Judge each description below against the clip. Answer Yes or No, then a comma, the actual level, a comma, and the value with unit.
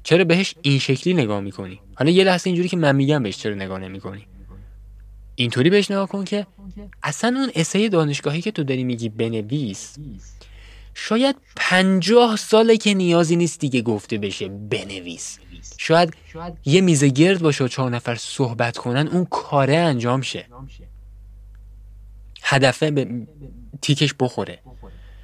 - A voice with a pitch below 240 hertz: Yes, low, 135 Hz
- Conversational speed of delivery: Yes, average, 140 wpm